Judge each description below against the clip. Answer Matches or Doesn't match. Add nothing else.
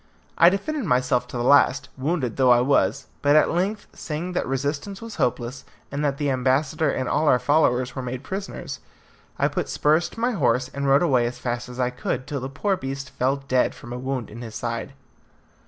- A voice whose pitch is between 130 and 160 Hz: Matches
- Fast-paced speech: Matches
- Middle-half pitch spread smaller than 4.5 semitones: Matches